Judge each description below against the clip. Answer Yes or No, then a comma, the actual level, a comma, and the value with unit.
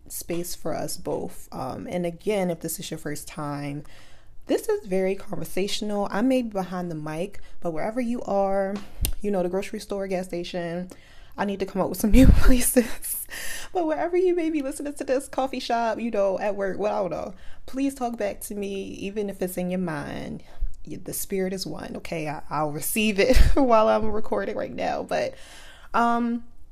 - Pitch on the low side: No, high, 200 Hz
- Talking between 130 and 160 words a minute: No, average, 200 wpm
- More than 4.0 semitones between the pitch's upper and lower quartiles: Yes, average, 4.8 semitones